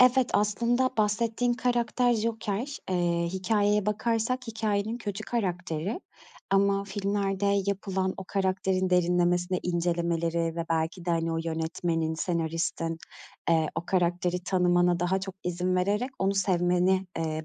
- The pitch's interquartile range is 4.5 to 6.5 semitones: No, average, 3.3 semitones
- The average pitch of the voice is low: No, medium, 185 Hz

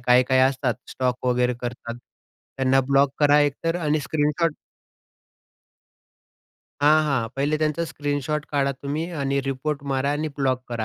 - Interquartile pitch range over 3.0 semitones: No, narrow, 2.5 semitones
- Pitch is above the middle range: No, medium, 140 Hz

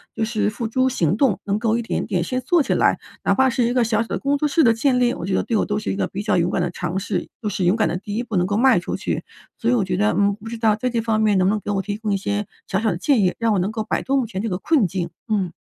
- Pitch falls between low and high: No, high, 215 Hz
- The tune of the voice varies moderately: Yes, average, 3.4 semitones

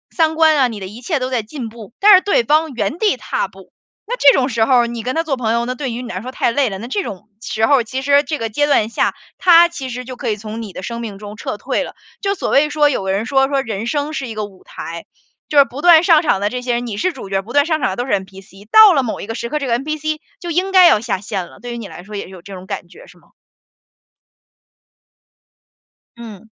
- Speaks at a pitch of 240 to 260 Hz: Yes, high, 245 Hz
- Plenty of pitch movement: Yes, wide, 5.8 semitones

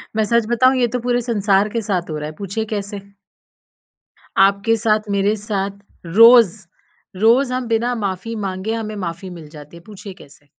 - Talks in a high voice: Yes, high, 210 Hz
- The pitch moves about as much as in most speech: Yes, average, 3.1 semitones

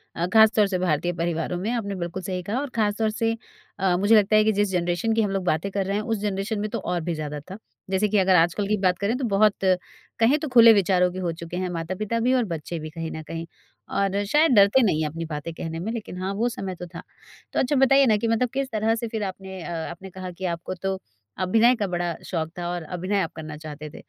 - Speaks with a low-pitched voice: No, high, 190 Hz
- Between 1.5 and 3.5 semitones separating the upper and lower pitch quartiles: No, average, 3.9 semitones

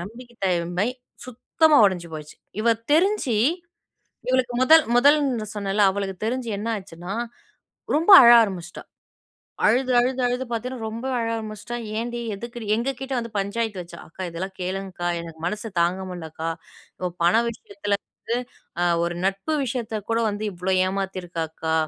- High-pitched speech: Yes, high, 210 Hz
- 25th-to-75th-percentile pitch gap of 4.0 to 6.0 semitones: Yes, average, 4.8 semitones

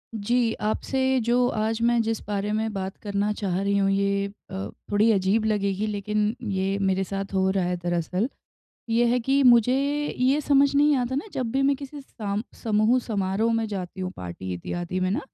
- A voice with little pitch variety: No, average, 3.8 semitones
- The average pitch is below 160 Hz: No, high, 210 Hz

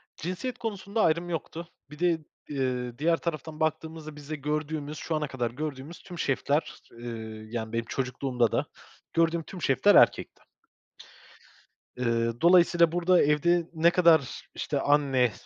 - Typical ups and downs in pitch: Yes, average, 4.6 semitones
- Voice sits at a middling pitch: Yes, medium, 150 Hz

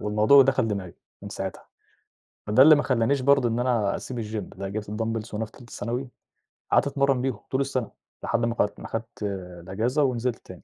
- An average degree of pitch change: Yes, average, 3.6 semitones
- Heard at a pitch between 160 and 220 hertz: No, low, 115 Hz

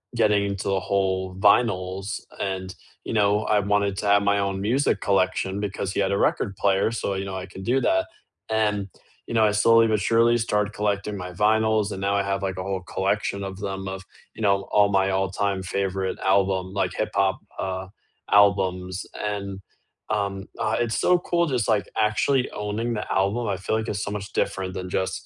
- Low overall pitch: Yes, low, 100 Hz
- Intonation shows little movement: Yes, narrow, 1.7 semitones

